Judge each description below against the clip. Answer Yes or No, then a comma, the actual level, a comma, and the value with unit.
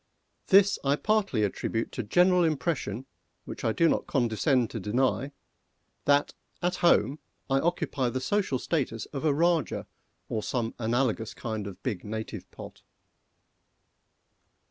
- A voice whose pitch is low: Yes, low, 130 Hz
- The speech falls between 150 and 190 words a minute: No, slow, 135 wpm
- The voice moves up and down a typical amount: No, wide, 6.5 semitones